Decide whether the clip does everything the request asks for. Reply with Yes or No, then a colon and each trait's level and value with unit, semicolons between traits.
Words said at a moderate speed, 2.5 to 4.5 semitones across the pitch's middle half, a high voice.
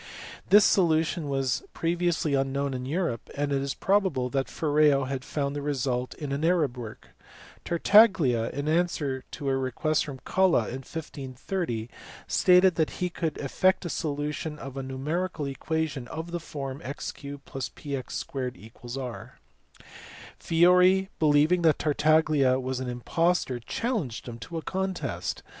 No: average, 145 wpm; average, 4.1 semitones; medium, 145 Hz